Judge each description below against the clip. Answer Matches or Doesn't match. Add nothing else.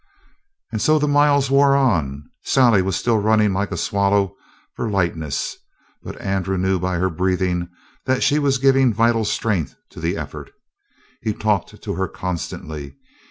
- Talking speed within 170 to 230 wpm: Doesn't match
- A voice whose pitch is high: Doesn't match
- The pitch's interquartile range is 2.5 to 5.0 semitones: Doesn't match